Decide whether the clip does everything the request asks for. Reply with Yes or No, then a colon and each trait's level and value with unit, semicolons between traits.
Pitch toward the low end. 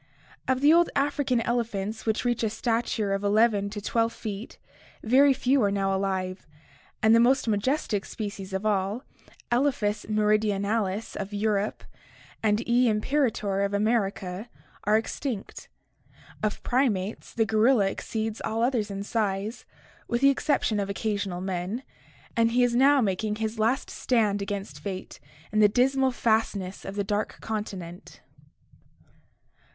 No: high, 215 Hz